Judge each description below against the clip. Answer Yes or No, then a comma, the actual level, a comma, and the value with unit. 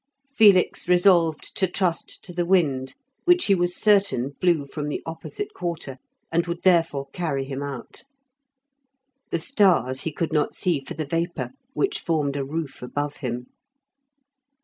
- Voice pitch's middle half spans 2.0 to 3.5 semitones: No, average, 4.2 semitones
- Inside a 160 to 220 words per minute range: No, average, 150 wpm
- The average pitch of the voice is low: No, medium, 165 Hz